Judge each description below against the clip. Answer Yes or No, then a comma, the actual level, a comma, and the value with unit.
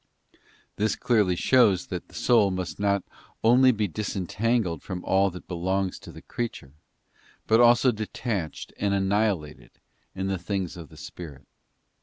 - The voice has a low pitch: Yes, low, 100 Hz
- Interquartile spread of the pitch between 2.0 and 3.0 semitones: No, average, 3.5 semitones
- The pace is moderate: Yes, average, 145 wpm